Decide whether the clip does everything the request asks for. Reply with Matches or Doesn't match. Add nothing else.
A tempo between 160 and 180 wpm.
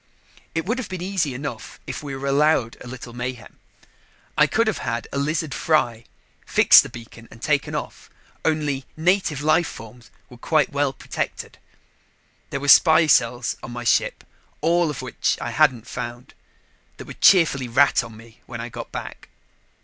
Matches